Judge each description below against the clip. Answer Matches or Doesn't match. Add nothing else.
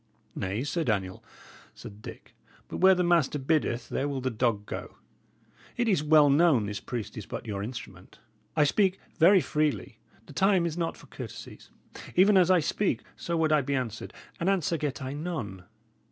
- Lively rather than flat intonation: Matches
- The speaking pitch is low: Doesn't match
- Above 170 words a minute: Matches